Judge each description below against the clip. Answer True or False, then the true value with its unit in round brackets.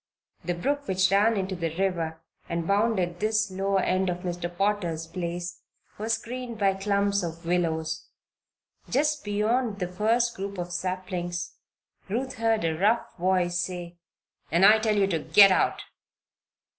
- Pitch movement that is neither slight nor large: True (3.3 semitones)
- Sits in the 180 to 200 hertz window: True (190 Hz)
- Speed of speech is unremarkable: True (150 wpm)